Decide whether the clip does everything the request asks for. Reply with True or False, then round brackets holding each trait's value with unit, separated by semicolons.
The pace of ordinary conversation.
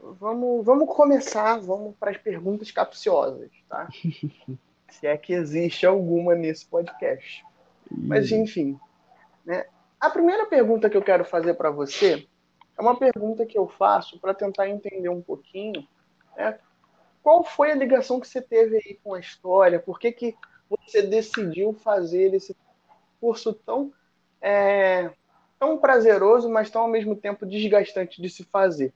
True (150 wpm)